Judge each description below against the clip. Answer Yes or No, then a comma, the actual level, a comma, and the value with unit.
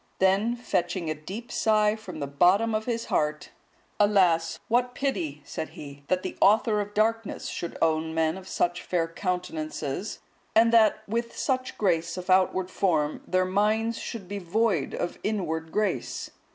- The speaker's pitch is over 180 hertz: Yes, high, 190 Hz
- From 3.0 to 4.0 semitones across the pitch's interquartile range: No, average, 4.8 semitones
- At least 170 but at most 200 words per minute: No, average, 160 wpm